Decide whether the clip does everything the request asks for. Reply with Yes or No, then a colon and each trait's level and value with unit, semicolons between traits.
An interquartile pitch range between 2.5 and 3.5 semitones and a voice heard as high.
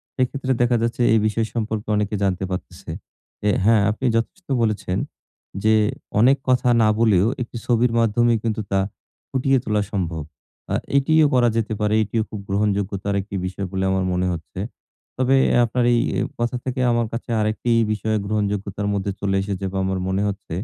No: average, 3.2 semitones; low, 110 Hz